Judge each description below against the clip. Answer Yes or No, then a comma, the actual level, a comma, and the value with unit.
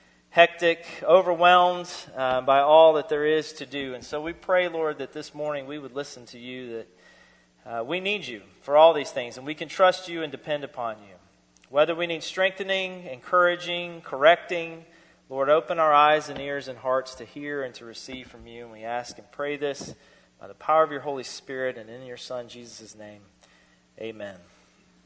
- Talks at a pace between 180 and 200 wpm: Yes, average, 195 wpm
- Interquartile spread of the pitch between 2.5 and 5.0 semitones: No, wide, 5.5 semitones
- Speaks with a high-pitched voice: No, medium, 140 Hz